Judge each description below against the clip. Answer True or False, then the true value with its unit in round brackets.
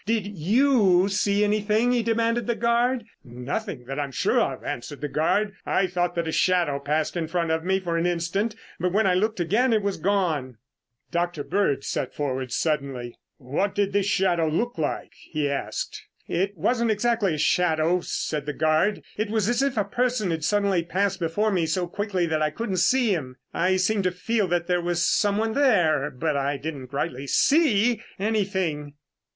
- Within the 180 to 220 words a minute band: True (190 wpm)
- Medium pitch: True (180 Hz)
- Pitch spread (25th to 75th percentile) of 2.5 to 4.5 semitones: False (5.2 semitones)